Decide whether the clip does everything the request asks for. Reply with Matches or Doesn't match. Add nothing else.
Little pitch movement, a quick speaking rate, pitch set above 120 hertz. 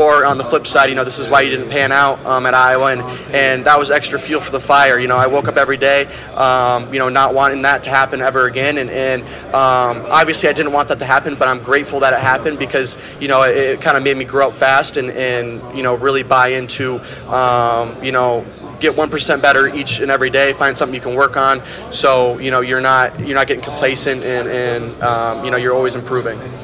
Matches